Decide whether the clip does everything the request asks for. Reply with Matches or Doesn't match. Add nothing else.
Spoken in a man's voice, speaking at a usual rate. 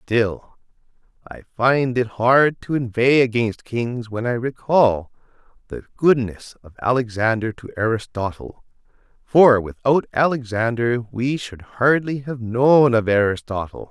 Doesn't match